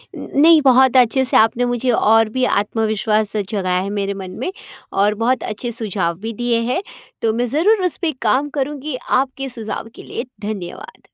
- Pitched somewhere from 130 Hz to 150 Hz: No, high, 230 Hz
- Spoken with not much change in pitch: No, average, 3.8 semitones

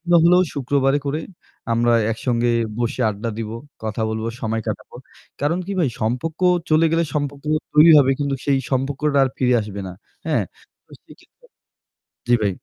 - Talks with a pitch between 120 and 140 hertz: Yes, low, 135 Hz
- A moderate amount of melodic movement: Yes, average, 4.6 semitones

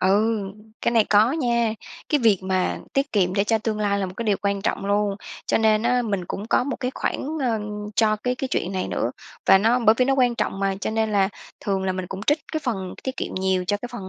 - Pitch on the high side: Yes, high, 215 Hz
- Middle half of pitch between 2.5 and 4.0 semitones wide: Yes, average, 3.5 semitones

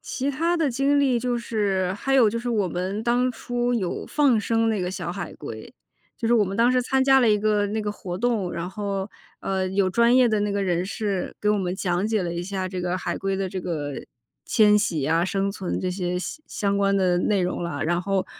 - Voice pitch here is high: Yes, high, 200 Hz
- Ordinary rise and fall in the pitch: Yes, average, 4.1 semitones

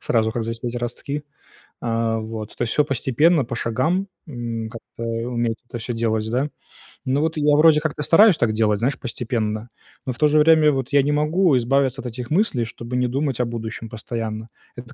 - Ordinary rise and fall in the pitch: Yes, average, 4.2 semitones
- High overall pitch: No, low, 120 Hz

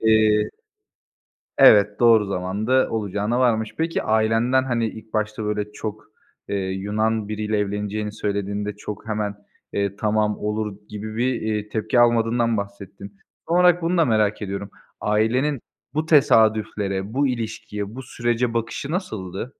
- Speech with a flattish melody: Yes, narrow, 2.2 semitones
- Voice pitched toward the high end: No, low, 110 Hz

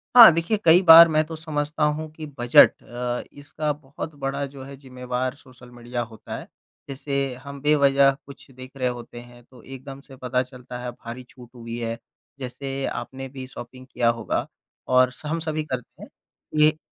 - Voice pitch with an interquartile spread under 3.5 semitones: Yes, average, 3.1 semitones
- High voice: No, low, 135 Hz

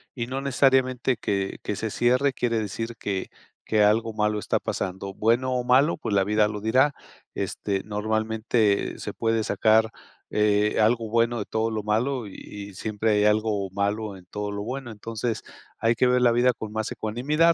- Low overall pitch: Yes, low, 110 Hz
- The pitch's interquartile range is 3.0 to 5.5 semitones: No, narrow, 2.6 semitones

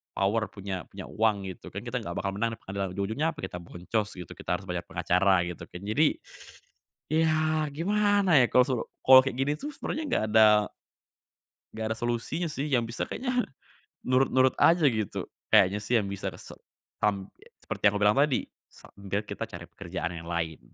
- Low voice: Yes, low, 110 Hz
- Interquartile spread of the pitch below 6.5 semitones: No, wide, 6.8 semitones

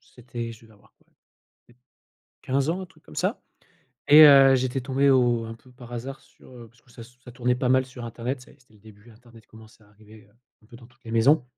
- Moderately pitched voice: No, low, 120 Hz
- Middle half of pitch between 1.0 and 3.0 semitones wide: Yes, narrow, 2.4 semitones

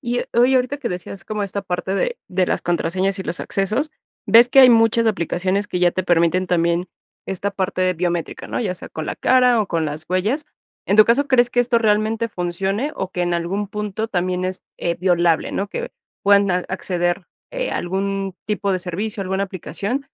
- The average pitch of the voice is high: Yes, high, 195 Hz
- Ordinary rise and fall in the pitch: Yes, average, 3.7 semitones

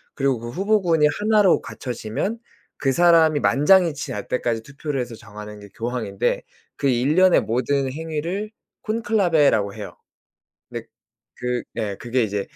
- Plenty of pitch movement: Yes, wide, 6.7 semitones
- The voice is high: No, medium, 140 Hz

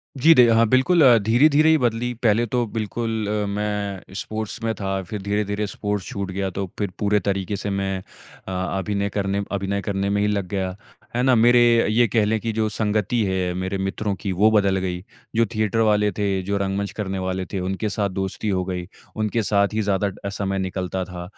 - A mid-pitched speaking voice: No, low, 100 Hz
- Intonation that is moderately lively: No, narrow, 2.1 semitones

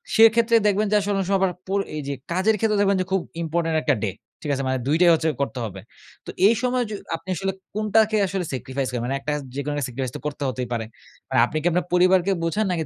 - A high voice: No, medium, 175 Hz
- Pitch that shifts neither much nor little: No, wide, 6.3 semitones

